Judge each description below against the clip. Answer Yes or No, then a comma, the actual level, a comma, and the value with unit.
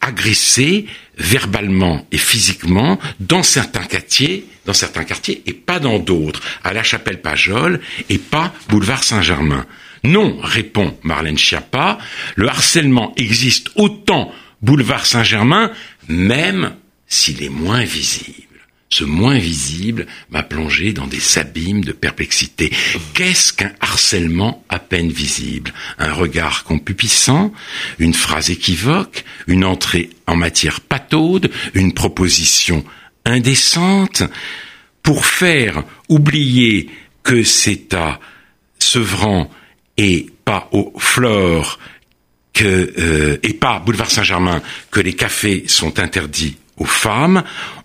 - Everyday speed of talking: No, slow, 115 wpm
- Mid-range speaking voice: No, low, 100 Hz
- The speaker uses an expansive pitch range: Yes, wide, 7.1 semitones